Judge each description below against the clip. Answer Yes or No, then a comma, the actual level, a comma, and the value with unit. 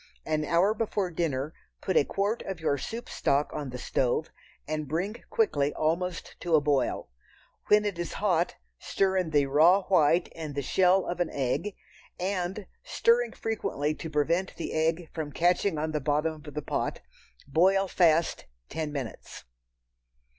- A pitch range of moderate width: Yes, average, 4.0 semitones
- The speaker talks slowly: No, average, 160 wpm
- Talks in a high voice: No, medium, 165 Hz